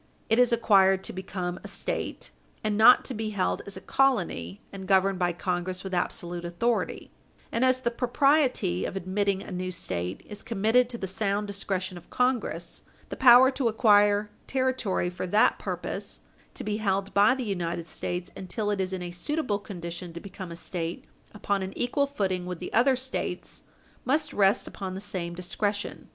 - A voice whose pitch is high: Yes, high, 200 Hz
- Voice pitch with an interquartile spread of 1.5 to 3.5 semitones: No, average, 4.2 semitones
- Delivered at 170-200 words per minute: Yes, average, 180 wpm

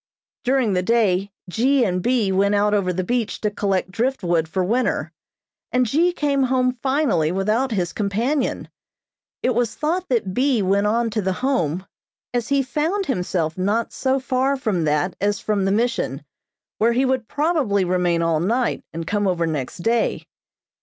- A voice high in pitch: Yes, high, 215 Hz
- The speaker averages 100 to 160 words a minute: No, average, 170 wpm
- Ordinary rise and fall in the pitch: No, wide, 5.7 semitones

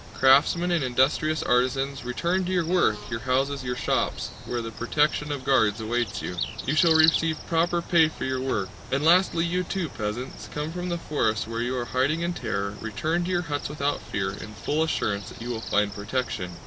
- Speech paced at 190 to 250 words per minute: Yes, average, 200 wpm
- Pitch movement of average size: No, wide, 5.7 semitones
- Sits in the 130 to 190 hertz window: Yes, low, 135 Hz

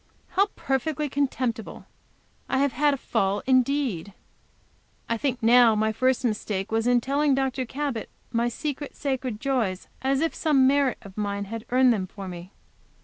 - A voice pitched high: Yes, very high, 250 Hz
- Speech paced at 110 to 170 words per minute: Yes, average, 160 wpm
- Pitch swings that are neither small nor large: Yes, average, 4.0 semitones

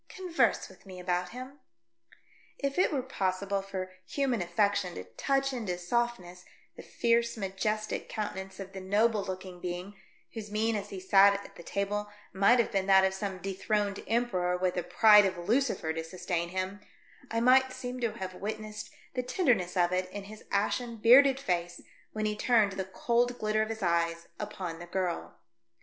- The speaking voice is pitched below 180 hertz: No, high, 200 Hz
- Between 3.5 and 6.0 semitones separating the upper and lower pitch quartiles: Yes, average, 3.8 semitones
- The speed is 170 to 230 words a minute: Yes, average, 180 wpm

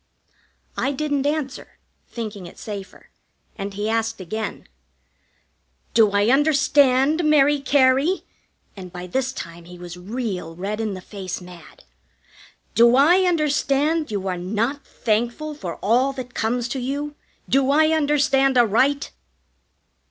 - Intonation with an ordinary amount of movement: No, wide, 6.0 semitones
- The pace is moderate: No, slow, 130 wpm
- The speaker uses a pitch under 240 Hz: No, high, 245 Hz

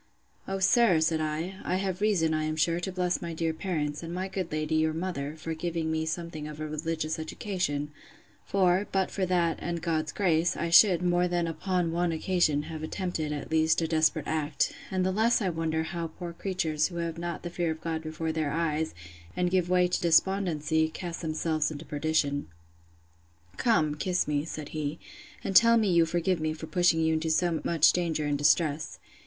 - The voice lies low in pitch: No, medium, 165 Hz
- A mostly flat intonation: Yes, narrow, 2.2 semitones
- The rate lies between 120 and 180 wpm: No, average, 200 wpm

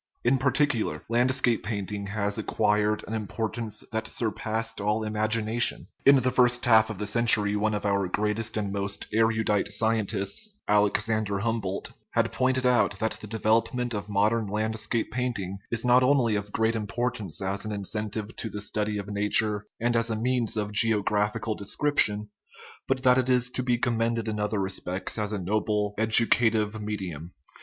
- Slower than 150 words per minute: No, average, 170 wpm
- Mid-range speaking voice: No, low, 110 Hz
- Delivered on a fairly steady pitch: Yes, narrow, 2.1 semitones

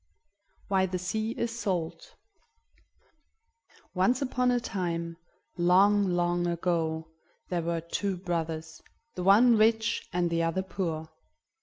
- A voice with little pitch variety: No, average, 3.4 semitones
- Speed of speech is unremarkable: No, slow, 120 wpm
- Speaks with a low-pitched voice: No, medium, 180 Hz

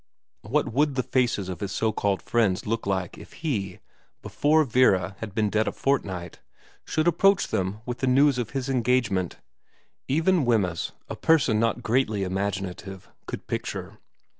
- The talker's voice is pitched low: Yes, low, 115 Hz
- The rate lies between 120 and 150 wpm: No, average, 160 wpm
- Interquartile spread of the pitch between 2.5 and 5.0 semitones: No, wide, 5.5 semitones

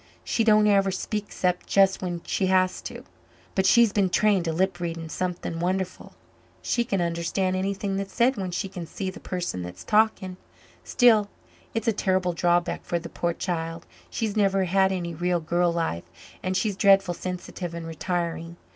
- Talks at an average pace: Yes, average, 175 wpm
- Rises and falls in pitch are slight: Yes, narrow, 2.3 semitones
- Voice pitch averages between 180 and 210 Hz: Yes, medium, 185 Hz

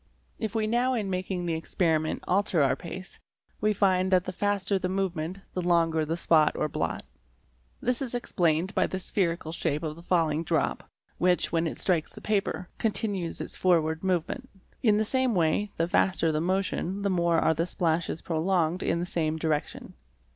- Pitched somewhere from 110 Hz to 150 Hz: No, medium, 180 Hz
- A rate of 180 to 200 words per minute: Yes, average, 185 wpm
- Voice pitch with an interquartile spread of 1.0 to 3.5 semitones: Yes, average, 3.1 semitones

